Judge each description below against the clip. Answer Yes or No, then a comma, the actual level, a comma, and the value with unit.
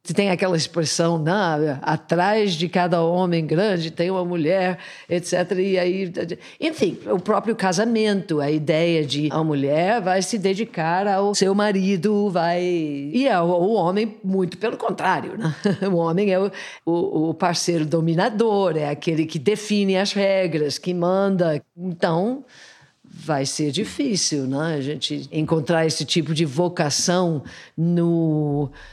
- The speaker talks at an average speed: Yes, average, 140 wpm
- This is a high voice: No, medium, 175 Hz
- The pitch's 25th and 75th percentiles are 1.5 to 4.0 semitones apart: Yes, average, 3.4 semitones